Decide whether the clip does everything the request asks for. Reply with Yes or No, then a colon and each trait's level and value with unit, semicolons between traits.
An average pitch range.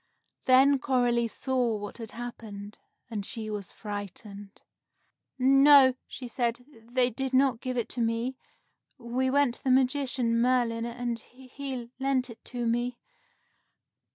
No: narrow, 2.2 semitones